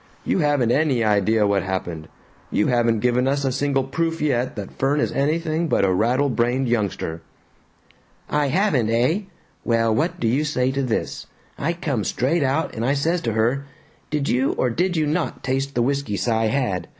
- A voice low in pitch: Yes, low, 130 Hz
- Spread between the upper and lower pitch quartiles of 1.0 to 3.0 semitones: No, average, 4.4 semitones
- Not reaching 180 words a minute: No, average, 185 wpm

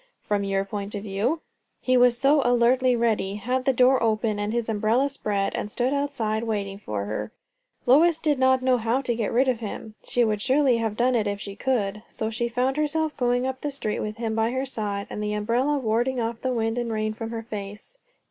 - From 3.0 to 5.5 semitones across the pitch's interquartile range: Yes, average, 3.5 semitones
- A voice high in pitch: Yes, high, 235 Hz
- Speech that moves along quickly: Yes, fast, 225 wpm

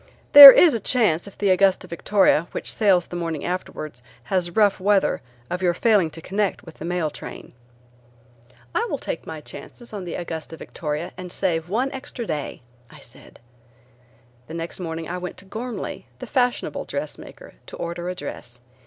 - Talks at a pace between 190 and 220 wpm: No, average, 175 wpm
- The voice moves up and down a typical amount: Yes, average, 3.9 semitones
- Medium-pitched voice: Yes, medium, 180 Hz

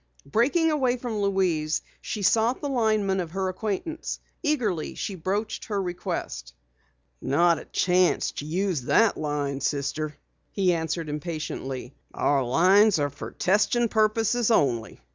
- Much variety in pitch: Yes, wide, 6.2 semitones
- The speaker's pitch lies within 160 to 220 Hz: Yes, medium, 185 Hz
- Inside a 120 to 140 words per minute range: Yes, slow, 135 wpm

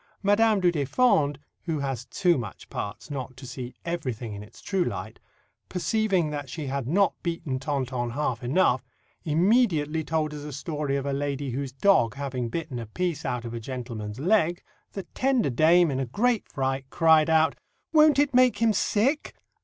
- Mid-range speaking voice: Yes, medium, 150 Hz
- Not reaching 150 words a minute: No, average, 175 wpm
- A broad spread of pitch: Yes, wide, 5.7 semitones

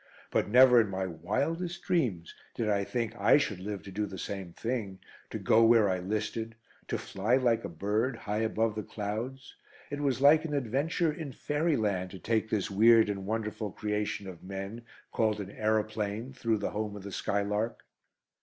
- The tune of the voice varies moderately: Yes, average, 3.2 semitones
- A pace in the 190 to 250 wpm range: No, average, 180 wpm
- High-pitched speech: No, low, 110 Hz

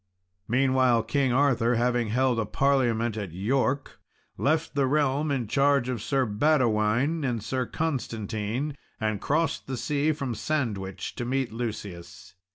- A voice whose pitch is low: Yes, low, 130 Hz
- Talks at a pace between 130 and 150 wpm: Yes, average, 140 wpm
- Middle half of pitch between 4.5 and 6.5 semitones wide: No, average, 3.8 semitones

